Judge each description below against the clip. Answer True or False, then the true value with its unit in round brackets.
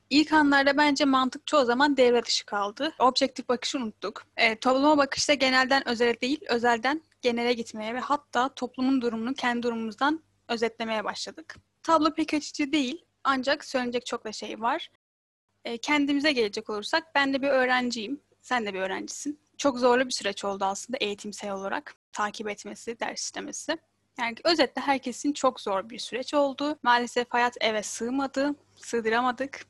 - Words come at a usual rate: False (155 wpm)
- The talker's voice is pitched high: True (255 Hz)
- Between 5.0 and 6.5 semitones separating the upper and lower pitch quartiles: False (3.4 semitones)